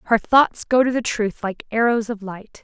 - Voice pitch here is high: Yes, high, 225 Hz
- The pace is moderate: No, fast, 230 wpm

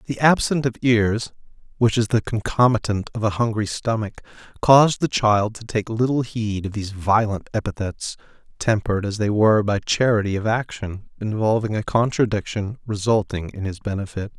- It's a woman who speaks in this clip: No, male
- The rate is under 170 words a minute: Yes, average, 160 wpm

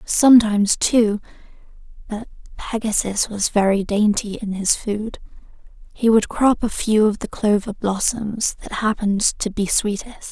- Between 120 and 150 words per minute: Yes, average, 140 wpm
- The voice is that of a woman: Yes, female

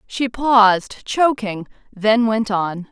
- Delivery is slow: Yes, slow, 125 wpm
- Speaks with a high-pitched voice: Yes, high, 220 Hz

